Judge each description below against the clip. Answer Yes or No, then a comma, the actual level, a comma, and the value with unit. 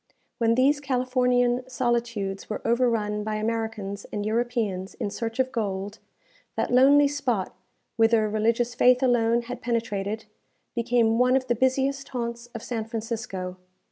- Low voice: No, high, 235 Hz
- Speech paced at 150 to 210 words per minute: No, average, 140 wpm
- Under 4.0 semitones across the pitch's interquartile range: Yes, narrow, 2.5 semitones